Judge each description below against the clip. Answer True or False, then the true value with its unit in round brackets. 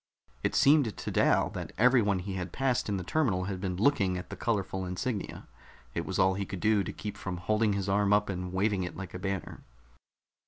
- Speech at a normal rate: False (220 wpm)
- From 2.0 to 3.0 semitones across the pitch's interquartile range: True (2.6 semitones)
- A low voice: True (100 Hz)